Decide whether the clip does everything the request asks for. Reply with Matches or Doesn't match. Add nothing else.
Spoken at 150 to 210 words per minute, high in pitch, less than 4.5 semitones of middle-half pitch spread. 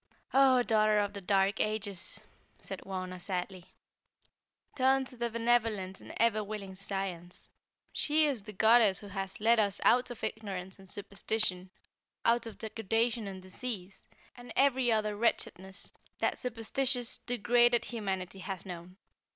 Doesn't match